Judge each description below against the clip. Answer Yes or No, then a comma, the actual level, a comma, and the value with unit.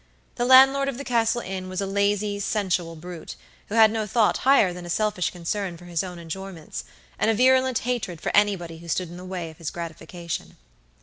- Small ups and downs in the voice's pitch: No, average, 4.4 semitones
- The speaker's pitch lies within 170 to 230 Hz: Yes, high, 190 Hz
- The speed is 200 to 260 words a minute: Yes, fast, 205 wpm